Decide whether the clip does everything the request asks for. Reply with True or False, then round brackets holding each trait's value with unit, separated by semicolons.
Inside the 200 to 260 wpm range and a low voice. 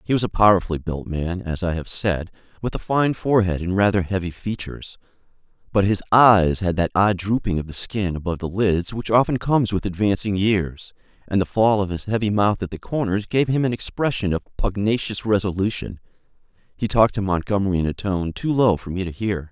True (205 wpm; 100 Hz)